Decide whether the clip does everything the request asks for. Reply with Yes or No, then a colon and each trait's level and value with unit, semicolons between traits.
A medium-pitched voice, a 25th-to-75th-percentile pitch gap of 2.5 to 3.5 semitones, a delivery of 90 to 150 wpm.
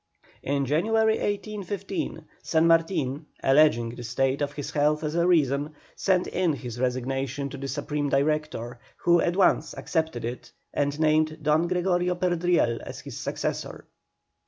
No: medium, 150 Hz; average, 4.1 semitones; average, 145 wpm